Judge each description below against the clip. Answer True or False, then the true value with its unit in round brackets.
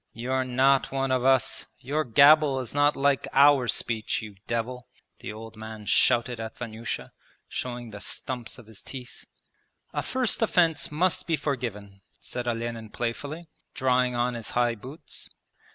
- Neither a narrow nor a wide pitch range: True (3.2 semitones)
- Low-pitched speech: True (125 Hz)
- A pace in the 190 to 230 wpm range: False (150 wpm)